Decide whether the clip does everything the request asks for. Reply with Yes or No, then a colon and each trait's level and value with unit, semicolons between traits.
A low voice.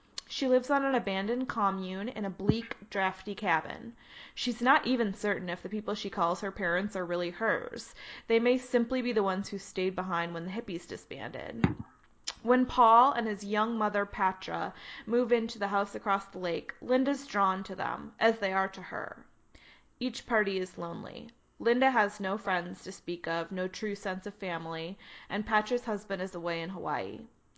No: high, 200 Hz